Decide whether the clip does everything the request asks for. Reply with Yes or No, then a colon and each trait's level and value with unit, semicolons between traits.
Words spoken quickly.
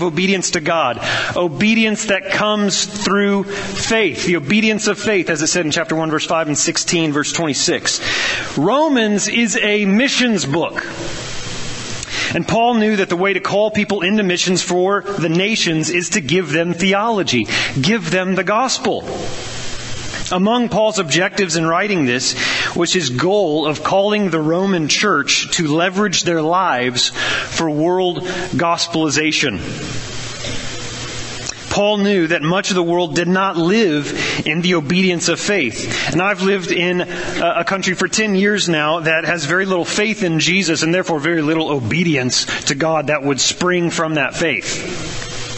No: average, 155 wpm